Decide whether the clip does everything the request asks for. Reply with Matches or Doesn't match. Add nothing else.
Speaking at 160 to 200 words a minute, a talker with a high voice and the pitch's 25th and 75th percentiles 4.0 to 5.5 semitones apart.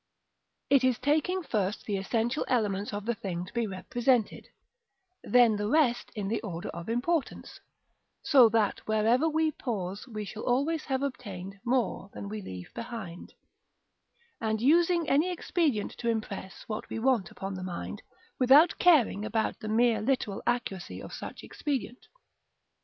Doesn't match